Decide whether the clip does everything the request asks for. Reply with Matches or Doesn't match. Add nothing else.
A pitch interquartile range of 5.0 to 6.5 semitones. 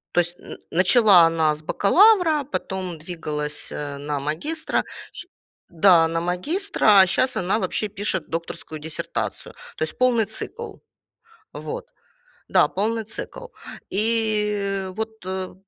Matches